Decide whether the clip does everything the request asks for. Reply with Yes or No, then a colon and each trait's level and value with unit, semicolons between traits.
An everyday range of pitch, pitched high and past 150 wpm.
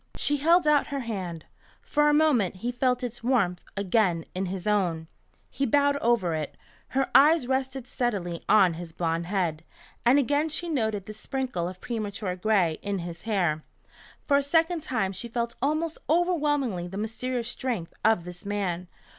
No: wide, 7.1 semitones; high, 225 Hz; average, 170 wpm